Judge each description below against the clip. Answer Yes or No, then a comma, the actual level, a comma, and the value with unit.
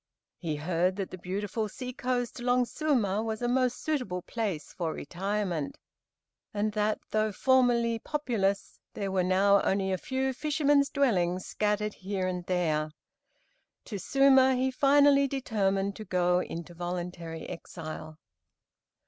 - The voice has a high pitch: Yes, high, 205 Hz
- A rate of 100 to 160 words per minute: Yes, slow, 135 wpm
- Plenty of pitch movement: Yes, wide, 5.7 semitones